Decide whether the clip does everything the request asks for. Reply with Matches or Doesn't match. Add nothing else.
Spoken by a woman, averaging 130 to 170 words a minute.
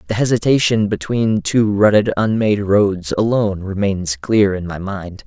Doesn't match